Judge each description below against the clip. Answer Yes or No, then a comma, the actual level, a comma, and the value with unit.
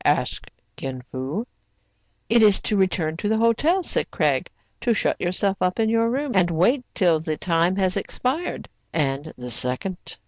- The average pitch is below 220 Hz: Yes, medium, 185 Hz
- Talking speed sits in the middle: Yes, average, 170 wpm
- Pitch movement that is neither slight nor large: No, wide, 6.2 semitones